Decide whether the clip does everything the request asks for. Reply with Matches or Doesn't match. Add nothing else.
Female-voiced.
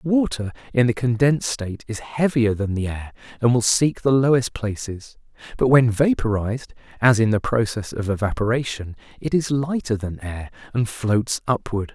Doesn't match